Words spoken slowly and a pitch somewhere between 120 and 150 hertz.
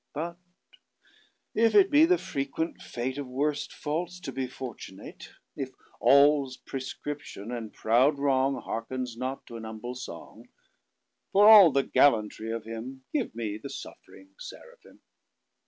Yes: slow, 120 wpm; low, 135 Hz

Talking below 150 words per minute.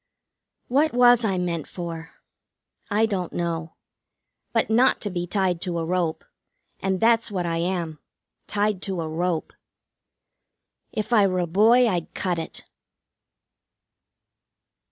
Yes: slow, 135 wpm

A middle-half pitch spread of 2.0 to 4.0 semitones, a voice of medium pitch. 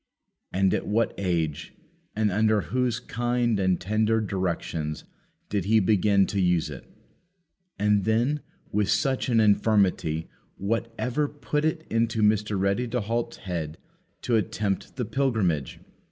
No: average, 3.7 semitones; low, 105 Hz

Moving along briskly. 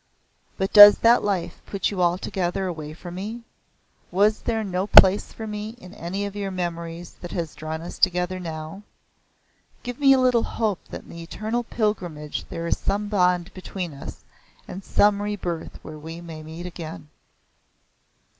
No: average, 165 wpm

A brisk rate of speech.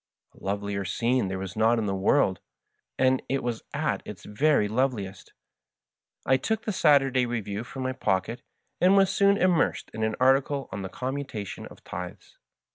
No: average, 180 wpm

